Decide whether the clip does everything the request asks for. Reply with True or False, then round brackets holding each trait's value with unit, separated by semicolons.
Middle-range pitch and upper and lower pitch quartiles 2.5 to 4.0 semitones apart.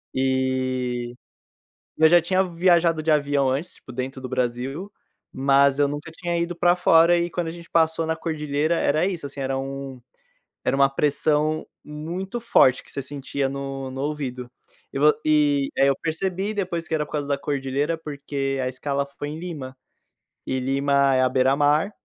True (145 Hz; 3.3 semitones)